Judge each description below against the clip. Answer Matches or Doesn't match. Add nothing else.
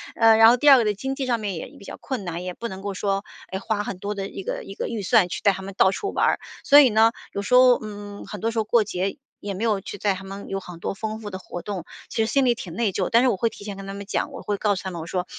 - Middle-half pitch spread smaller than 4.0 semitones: Matches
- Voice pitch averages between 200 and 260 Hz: Matches